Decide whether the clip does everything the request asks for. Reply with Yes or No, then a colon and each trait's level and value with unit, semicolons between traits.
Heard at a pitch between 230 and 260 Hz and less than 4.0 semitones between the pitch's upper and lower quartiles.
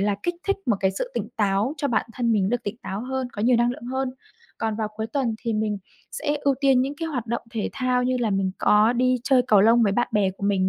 Yes: high, 235 Hz; average, 3.4 semitones